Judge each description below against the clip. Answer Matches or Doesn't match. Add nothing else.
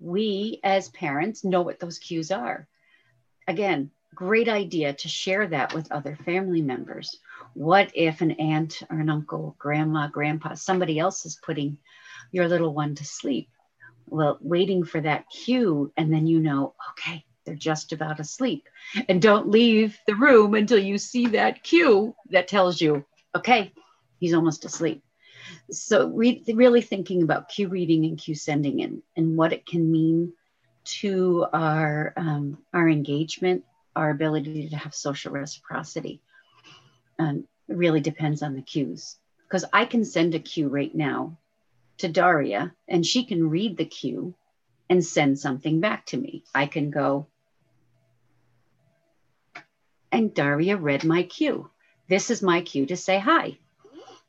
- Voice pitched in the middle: Matches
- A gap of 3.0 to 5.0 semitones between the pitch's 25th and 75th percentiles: Matches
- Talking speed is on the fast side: Doesn't match